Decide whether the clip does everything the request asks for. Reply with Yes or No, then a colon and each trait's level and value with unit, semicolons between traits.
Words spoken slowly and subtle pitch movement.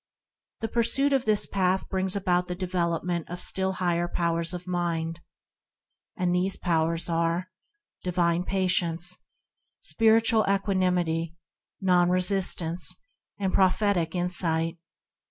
Yes: slow, 120 wpm; narrow, 2.0 semitones